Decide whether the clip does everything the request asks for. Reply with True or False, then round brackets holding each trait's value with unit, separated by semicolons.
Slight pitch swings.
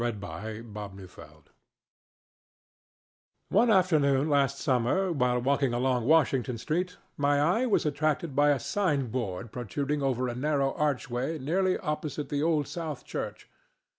False (3.9 semitones)